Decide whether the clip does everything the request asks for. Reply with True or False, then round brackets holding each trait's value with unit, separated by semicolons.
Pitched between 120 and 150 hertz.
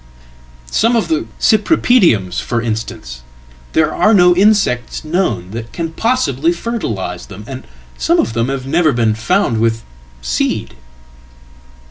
True (135 Hz)